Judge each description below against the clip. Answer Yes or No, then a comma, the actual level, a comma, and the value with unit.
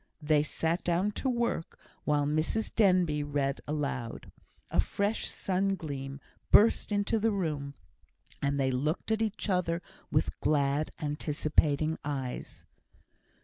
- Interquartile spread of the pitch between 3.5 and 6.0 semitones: Yes, average, 5.3 semitones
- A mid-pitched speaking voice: Yes, medium, 155 Hz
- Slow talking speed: Yes, slow, 125 wpm